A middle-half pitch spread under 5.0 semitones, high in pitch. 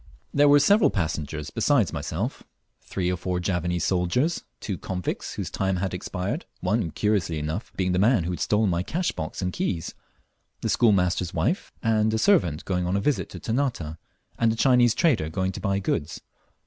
No: average, 4.4 semitones; very low, 95 Hz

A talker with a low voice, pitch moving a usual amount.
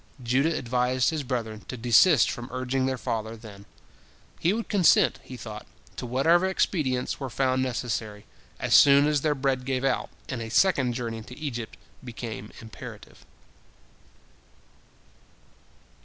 Yes: low, 125 Hz; average, 3.0 semitones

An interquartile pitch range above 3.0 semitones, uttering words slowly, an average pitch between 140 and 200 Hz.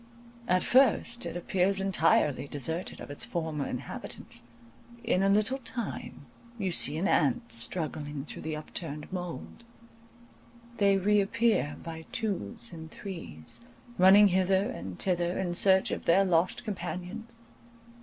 Yes: average, 3.9 semitones; slow, 130 wpm; medium, 185 Hz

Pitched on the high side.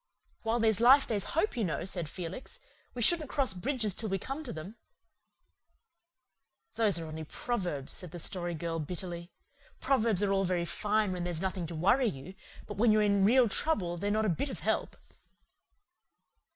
Yes: high, 195 Hz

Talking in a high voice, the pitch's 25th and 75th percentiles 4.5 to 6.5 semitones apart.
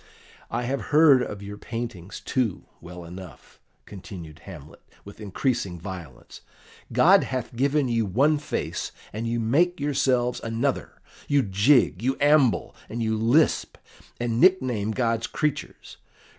No: low, 115 Hz; average, 5.2 semitones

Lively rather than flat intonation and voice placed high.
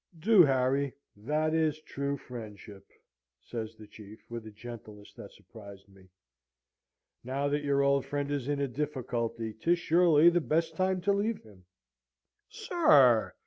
No: wide, 5.9 semitones; medium, 140 Hz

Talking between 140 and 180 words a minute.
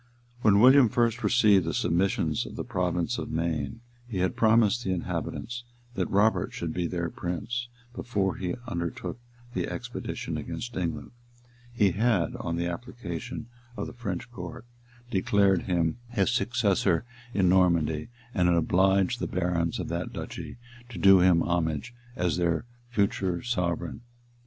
Yes: average, 150 wpm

